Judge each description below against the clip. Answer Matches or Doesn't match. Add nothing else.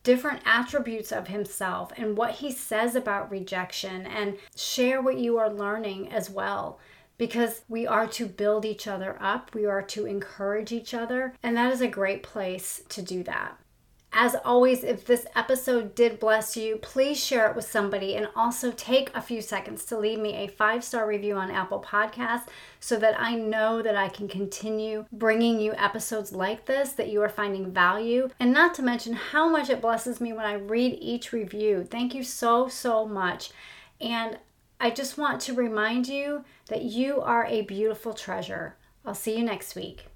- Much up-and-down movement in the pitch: Doesn't match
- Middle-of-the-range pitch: Doesn't match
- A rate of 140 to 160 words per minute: Doesn't match